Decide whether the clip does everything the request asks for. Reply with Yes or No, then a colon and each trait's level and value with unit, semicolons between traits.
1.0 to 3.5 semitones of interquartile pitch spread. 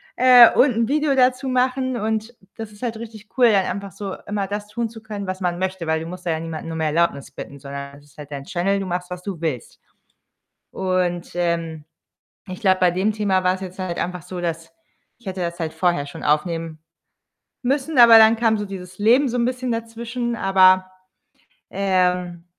No: average, 4.7 semitones